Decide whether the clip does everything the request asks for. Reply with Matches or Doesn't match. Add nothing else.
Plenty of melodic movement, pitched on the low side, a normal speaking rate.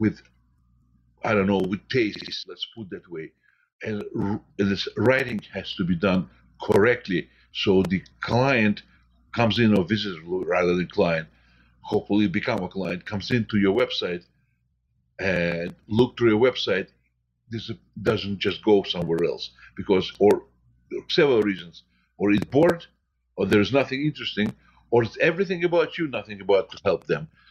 Matches